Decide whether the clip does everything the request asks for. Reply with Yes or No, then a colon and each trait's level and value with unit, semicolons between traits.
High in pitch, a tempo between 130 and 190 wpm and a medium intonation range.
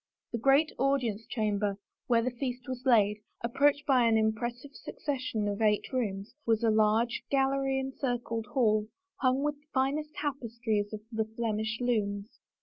Yes: high, 235 Hz; average, 150 wpm; average, 3.6 semitones